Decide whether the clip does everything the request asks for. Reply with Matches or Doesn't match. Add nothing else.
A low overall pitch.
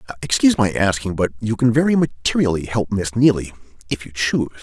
Matches